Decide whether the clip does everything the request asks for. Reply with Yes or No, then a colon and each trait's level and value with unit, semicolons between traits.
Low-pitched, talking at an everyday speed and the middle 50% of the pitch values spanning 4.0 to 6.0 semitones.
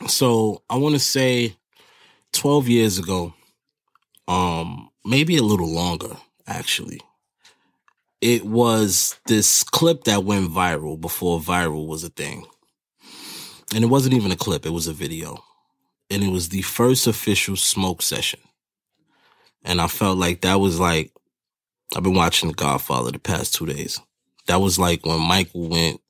Yes: very low, 95 Hz; average, 150 wpm; average, 4.8 semitones